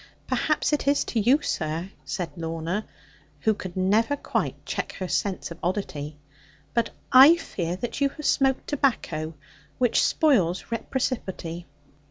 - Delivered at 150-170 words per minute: No, average, 140 wpm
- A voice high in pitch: Yes, high, 205 Hz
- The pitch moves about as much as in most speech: No, wide, 7.7 semitones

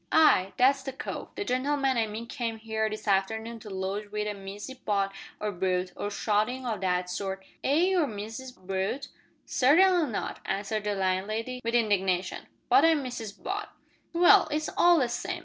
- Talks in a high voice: Yes, high, 220 Hz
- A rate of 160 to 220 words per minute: Yes, average, 175 wpm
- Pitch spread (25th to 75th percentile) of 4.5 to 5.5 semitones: Yes, average, 5.0 semitones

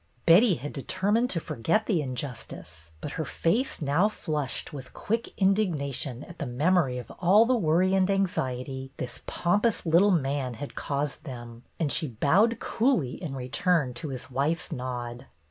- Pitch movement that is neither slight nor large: No, wide, 6.5 semitones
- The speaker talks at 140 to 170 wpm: No, average, 180 wpm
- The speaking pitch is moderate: Yes, medium, 150 Hz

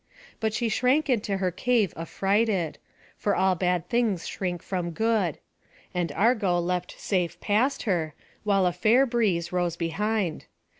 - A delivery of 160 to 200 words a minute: No, average, 145 wpm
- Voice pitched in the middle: No, high, 195 Hz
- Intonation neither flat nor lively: Yes, average, 4.0 semitones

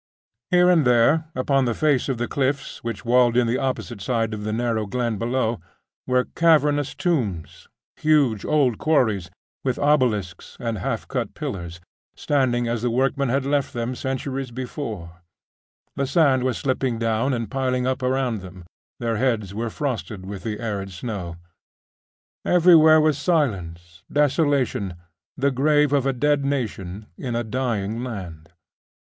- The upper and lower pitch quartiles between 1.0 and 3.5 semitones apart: No, average, 4.2 semitones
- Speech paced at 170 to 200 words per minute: No, average, 150 wpm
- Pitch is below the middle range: Yes, low, 125 Hz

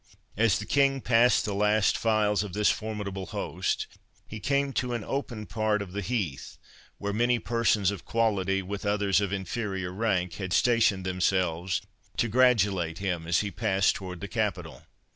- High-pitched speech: No, low, 100 Hz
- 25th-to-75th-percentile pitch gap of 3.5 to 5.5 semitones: No, average, 3.1 semitones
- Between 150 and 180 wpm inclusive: Yes, average, 165 wpm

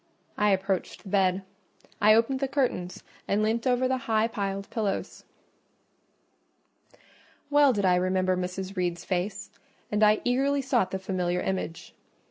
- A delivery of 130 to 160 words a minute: Yes, average, 140 wpm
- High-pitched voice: Yes, high, 200 Hz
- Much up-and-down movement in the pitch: No, average, 3.9 semitones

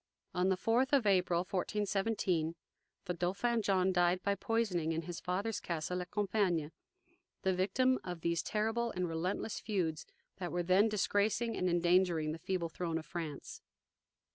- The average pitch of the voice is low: No, medium, 185 Hz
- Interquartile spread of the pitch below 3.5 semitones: Yes, average, 3.1 semitones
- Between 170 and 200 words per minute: No, average, 155 wpm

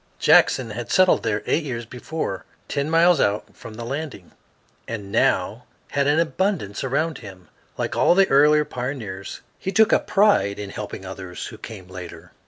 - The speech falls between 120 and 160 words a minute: No, average, 170 wpm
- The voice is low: Yes, low, 125 Hz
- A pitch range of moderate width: No, wide, 7.8 semitones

